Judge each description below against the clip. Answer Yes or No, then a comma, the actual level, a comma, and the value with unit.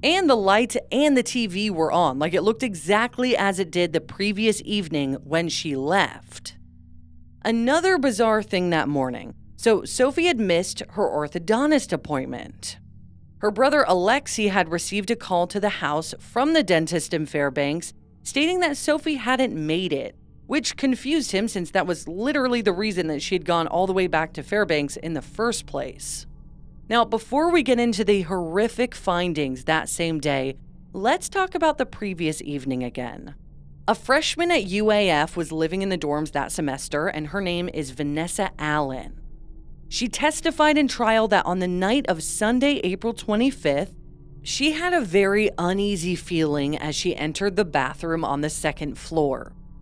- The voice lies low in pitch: No, medium, 185 Hz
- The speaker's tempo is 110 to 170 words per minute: Yes, average, 165 wpm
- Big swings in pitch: Yes, wide, 7.3 semitones